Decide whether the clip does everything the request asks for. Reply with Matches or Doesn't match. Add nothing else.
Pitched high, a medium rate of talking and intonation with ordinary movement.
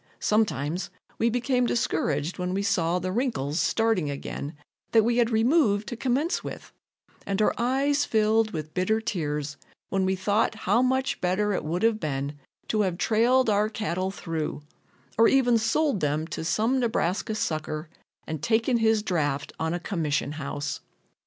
Doesn't match